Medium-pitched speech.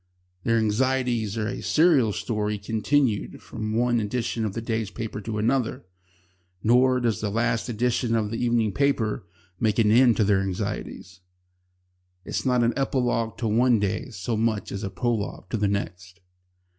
No: low, 115 Hz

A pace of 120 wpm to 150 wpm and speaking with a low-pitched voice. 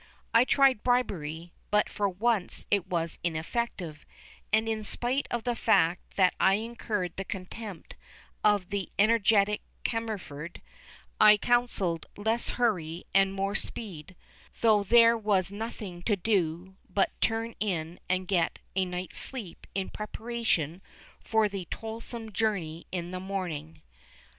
No: slow, 135 wpm; high, 200 Hz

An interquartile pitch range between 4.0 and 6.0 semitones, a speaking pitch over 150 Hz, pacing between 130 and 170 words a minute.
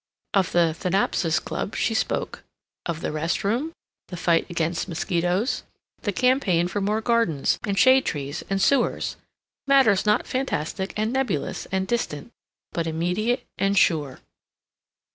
Yes: average, 5.1 semitones; high, 190 Hz; average, 140 wpm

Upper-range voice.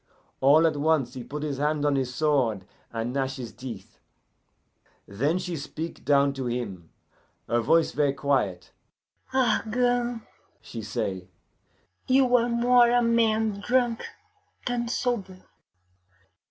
No: medium, 150 Hz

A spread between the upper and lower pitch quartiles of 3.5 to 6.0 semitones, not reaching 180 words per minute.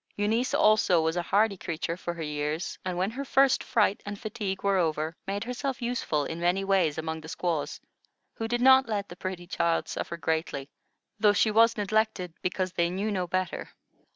No: average, 4.3 semitones; average, 190 wpm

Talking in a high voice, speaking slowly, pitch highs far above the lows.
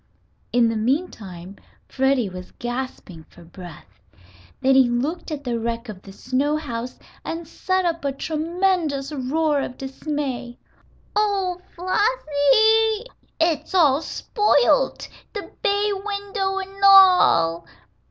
Yes: very high, 295 Hz; slow, 120 wpm; wide, 7.8 semitones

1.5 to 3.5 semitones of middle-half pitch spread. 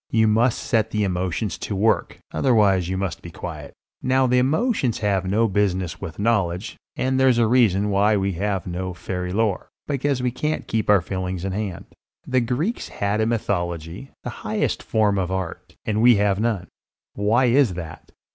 No: average, 4.1 semitones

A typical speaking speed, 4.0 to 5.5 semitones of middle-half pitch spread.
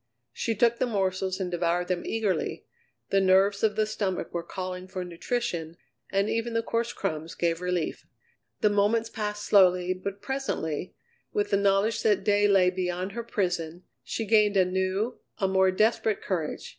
No: average, 170 wpm; average, 2.8 semitones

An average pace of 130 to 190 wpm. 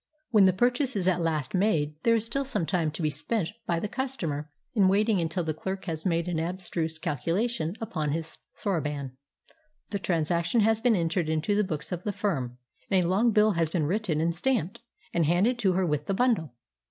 No: fast, 205 wpm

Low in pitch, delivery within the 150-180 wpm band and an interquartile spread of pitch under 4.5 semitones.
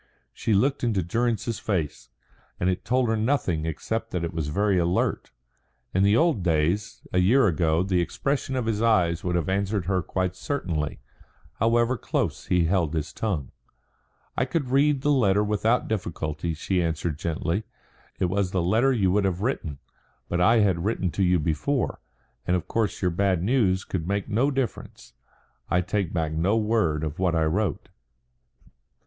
No: very low, 95 Hz; average, 175 wpm; average, 4.8 semitones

